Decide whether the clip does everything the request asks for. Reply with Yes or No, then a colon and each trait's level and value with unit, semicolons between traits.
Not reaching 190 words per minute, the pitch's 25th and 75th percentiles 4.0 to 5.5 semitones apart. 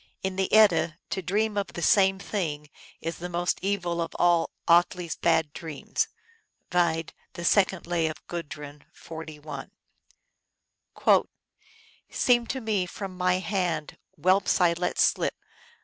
No: average, 140 wpm; average, 2.8 semitones